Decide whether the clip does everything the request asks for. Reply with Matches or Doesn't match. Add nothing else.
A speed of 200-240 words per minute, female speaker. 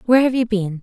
Doesn't match